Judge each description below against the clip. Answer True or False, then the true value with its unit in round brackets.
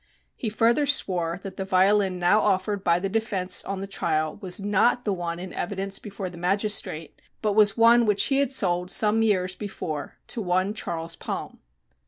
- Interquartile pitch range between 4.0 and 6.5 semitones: False (2.8 semitones)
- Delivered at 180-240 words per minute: True (185 wpm)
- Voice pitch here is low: False (195 Hz)